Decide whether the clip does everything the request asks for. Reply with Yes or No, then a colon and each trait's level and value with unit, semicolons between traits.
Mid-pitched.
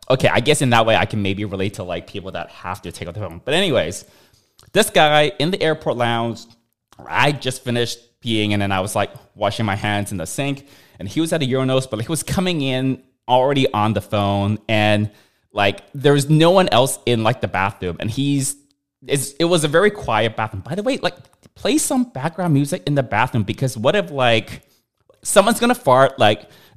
No: low, 120 Hz